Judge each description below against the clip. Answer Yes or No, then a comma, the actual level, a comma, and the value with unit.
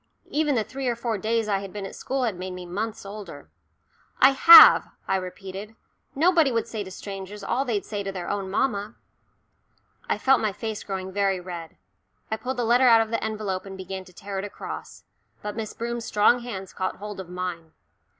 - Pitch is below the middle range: No, high, 205 Hz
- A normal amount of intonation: Yes, average, 3.4 semitones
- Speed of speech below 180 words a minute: No, fast, 205 wpm